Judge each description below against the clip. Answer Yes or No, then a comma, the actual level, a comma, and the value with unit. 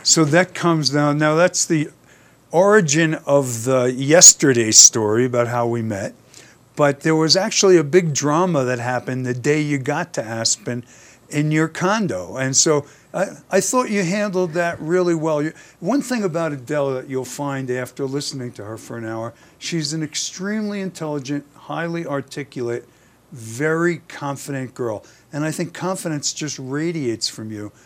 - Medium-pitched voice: Yes, medium, 145 Hz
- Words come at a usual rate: Yes, average, 165 wpm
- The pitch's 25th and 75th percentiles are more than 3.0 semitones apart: Yes, average, 4.8 semitones